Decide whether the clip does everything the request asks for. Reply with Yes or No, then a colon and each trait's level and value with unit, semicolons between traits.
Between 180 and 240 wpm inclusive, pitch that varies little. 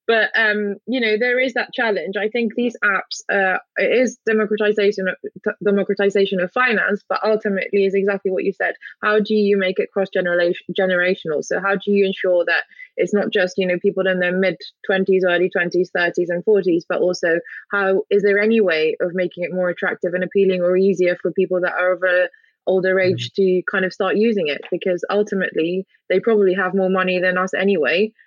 Yes: average, 200 wpm; narrow, 2.3 semitones